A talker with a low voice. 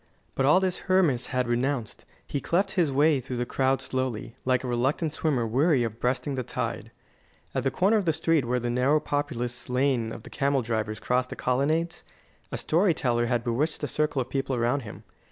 Yes: low, 130 Hz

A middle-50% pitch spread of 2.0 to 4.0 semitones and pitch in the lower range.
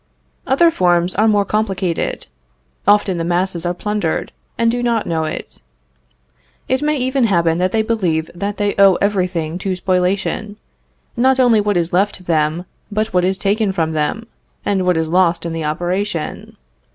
No: average, 3.6 semitones; high, 190 Hz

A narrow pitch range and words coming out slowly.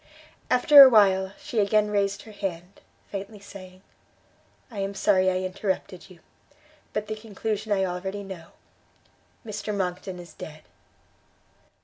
Yes: narrow, 2.1 semitones; slow, 130 wpm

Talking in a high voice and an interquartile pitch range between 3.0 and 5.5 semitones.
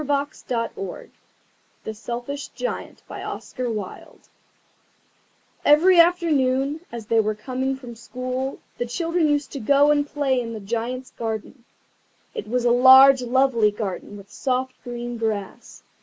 Yes: very high, 255 Hz; average, 3.4 semitones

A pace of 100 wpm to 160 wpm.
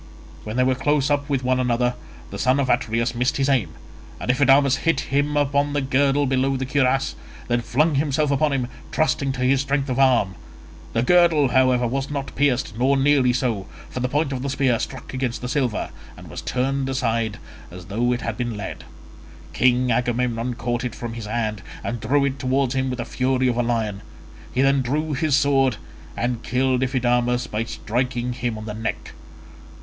No: average, 195 wpm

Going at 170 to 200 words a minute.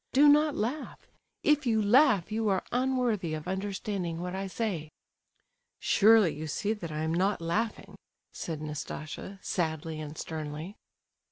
No: average, 145 wpm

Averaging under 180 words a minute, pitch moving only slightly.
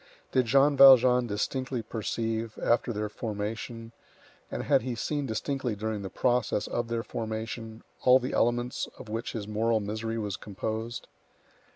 Yes: average, 150 wpm; narrow, 2.1 semitones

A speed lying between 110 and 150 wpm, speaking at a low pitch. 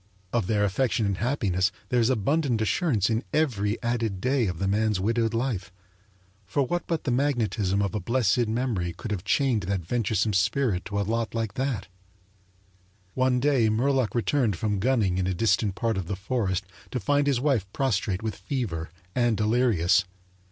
No: average, 175 wpm; low, 110 Hz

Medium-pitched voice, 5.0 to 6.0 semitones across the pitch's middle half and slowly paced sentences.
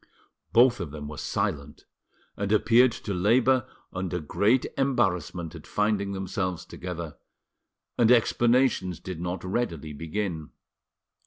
No: very low, 95 Hz; average, 5.3 semitones; slow, 115 wpm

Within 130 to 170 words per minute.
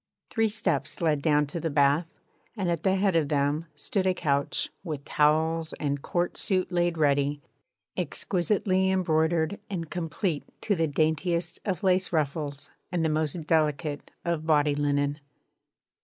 Yes: average, 150 wpm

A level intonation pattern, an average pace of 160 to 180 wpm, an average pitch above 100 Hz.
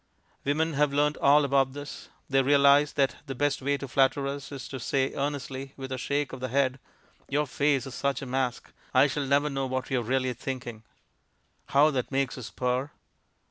No: narrow, 1.5 semitones; average, 195 wpm; low, 135 Hz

